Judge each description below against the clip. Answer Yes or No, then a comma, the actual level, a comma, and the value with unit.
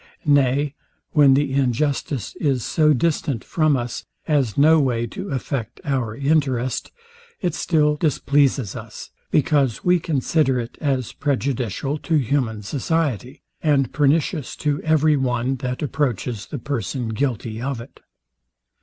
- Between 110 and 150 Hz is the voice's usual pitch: Yes, medium, 140 Hz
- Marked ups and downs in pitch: No, average, 3.3 semitones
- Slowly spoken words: Yes, slow, 130 wpm